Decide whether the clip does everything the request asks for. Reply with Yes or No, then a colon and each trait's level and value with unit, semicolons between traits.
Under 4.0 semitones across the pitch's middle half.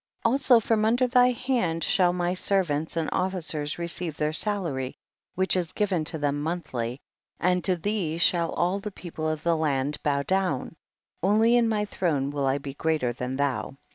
No: average, 5.1 semitones